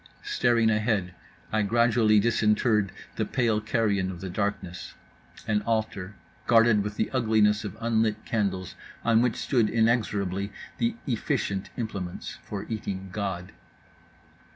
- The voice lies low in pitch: Yes, low, 105 Hz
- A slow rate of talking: Yes, slow, 120 wpm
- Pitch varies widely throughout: No, narrow, 2.5 semitones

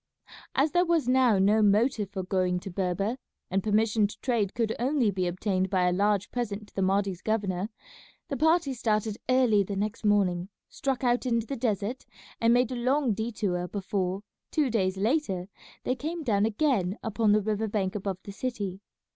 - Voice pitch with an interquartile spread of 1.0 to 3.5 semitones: No, average, 4.0 semitones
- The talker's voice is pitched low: No, high, 210 Hz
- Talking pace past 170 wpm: Yes, average, 180 wpm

